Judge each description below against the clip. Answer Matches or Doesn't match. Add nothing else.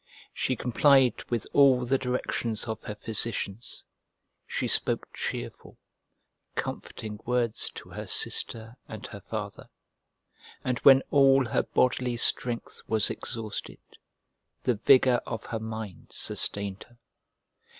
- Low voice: Matches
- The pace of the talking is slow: Matches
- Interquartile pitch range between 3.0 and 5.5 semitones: Doesn't match